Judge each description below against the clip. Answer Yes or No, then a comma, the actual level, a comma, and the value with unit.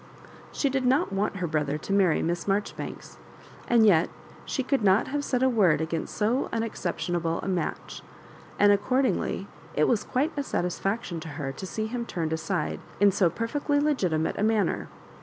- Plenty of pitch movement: Yes, wide, 6.1 semitones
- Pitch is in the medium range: No, high, 200 Hz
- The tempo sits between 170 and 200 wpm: Yes, average, 180 wpm